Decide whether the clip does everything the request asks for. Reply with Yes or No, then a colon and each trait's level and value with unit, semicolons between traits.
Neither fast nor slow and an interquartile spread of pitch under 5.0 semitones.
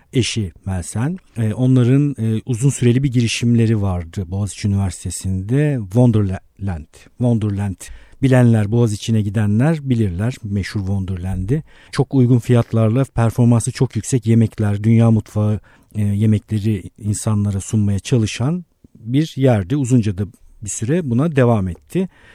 Yes: average, 105 wpm; average, 3.7 semitones